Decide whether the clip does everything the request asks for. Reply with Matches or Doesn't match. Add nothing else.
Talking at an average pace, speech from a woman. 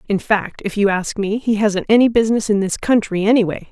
Doesn't match